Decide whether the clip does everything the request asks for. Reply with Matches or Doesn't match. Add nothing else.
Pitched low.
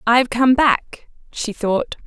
Doesn't match